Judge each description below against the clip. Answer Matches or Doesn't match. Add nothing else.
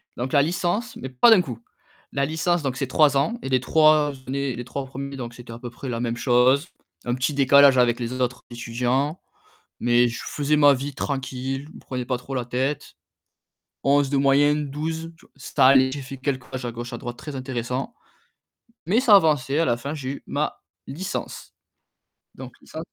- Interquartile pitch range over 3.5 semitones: Doesn't match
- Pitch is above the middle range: Doesn't match